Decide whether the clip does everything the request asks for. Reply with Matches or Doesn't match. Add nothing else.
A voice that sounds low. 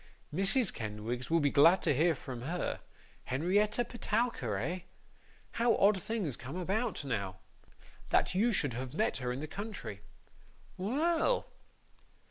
Doesn't match